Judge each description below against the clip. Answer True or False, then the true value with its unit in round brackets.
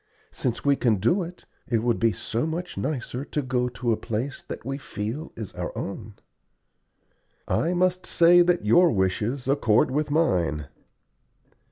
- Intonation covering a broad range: True (6.3 semitones)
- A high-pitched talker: False (125 Hz)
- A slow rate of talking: False (160 wpm)